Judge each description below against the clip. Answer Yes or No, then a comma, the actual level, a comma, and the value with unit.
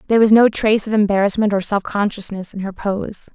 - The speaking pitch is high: Yes, high, 205 Hz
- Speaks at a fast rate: Yes, fast, 215 wpm